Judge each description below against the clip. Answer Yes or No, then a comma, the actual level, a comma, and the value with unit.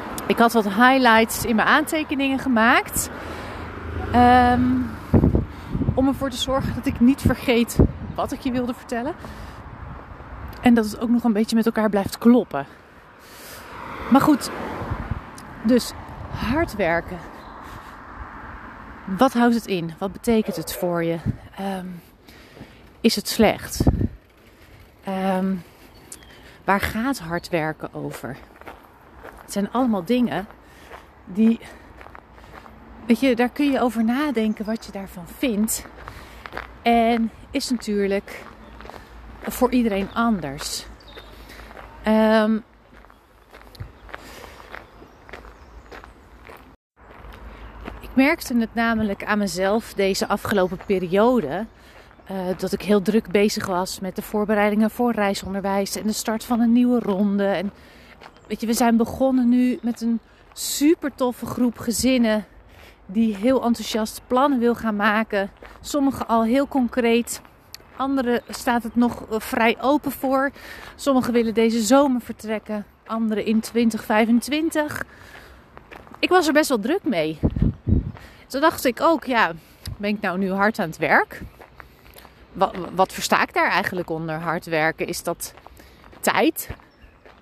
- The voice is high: Yes, high, 225 Hz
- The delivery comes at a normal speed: No, slow, 125 wpm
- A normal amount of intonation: Yes, average, 3.8 semitones